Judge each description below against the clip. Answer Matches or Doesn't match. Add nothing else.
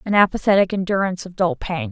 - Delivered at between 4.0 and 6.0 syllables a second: Doesn't match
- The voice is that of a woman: Matches